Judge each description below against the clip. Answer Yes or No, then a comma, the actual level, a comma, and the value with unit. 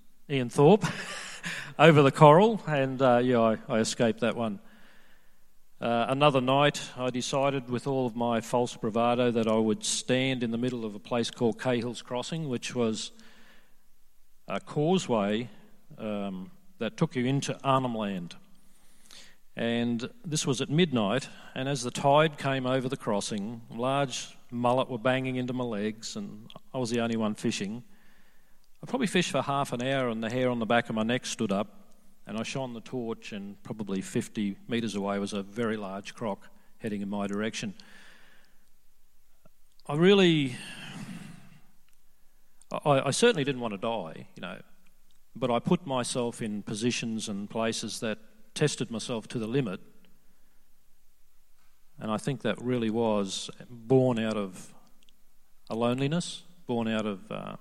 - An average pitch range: No, wide, 6.8 semitones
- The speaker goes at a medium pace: Yes, average, 160 wpm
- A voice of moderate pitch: No, low, 130 Hz